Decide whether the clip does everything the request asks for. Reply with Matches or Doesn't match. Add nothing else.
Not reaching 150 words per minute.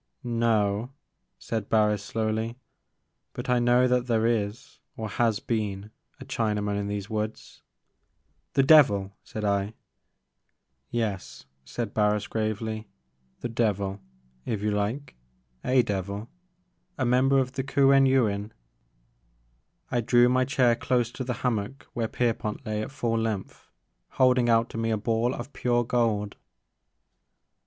Matches